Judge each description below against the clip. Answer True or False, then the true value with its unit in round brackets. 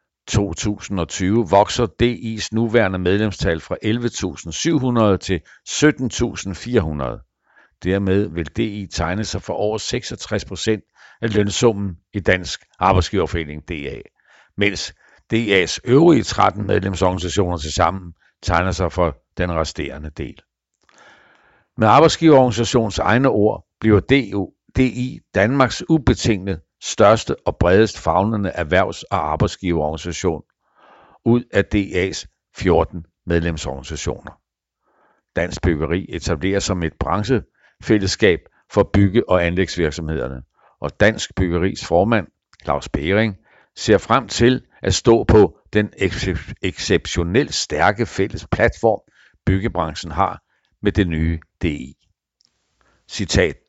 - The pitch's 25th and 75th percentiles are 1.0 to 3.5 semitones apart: False (4.5 semitones)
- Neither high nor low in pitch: False (95 Hz)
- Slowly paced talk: True (105 wpm)